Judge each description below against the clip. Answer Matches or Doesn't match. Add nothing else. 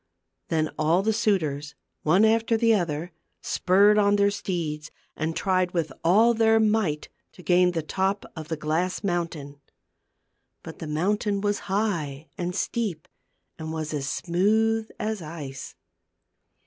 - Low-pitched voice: Doesn't match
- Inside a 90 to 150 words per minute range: Matches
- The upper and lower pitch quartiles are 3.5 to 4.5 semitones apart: Doesn't match